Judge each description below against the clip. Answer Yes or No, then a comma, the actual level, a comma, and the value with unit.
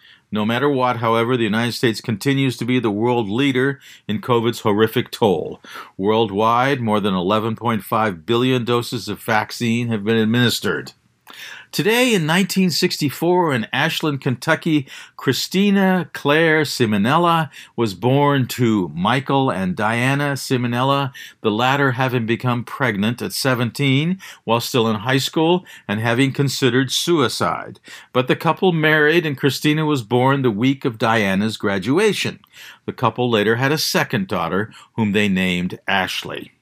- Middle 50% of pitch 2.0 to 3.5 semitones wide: No, average, 4.0 semitones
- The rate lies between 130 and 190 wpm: Yes, average, 140 wpm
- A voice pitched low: Yes, low, 125 Hz